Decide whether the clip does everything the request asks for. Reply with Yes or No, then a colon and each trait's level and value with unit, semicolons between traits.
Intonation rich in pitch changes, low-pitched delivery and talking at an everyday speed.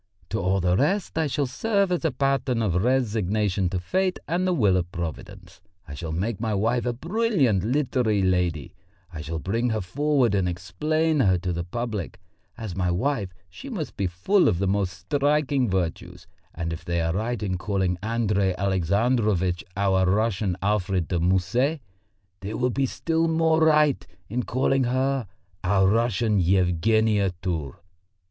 Yes: wide, 6.4 semitones; low, 105 Hz; average, 165 wpm